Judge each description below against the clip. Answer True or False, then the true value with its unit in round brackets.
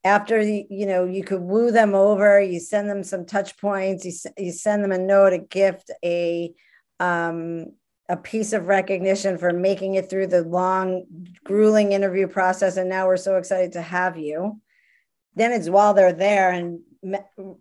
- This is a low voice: False (195 Hz)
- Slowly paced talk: False (180 wpm)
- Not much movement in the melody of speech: True (1.8 semitones)